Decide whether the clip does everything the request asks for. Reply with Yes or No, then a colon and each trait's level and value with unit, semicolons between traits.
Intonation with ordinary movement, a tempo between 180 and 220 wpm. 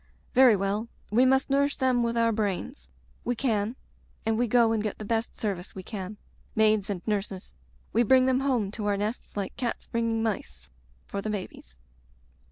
Yes: average, 3.1 semitones; average, 185 wpm